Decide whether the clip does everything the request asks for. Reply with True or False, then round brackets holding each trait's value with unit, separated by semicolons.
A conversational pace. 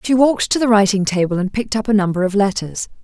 False (255 wpm)